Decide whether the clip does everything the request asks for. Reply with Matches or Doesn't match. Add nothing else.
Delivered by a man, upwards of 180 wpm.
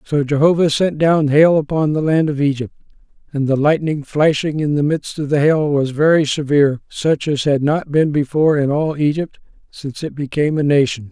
Matches